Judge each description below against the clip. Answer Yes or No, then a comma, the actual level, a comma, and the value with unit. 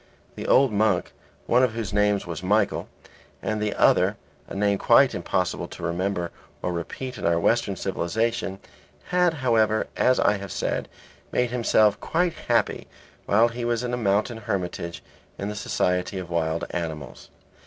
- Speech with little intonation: No, average, 4.5 semitones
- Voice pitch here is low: Yes, low, 105 Hz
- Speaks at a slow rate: No, average, 160 wpm